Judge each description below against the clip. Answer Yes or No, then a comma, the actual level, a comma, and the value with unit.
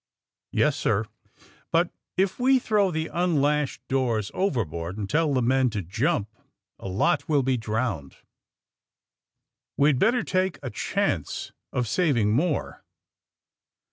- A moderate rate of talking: No, slow, 130 wpm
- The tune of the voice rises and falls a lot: Yes, wide, 8.1 semitones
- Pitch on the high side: No, low, 135 Hz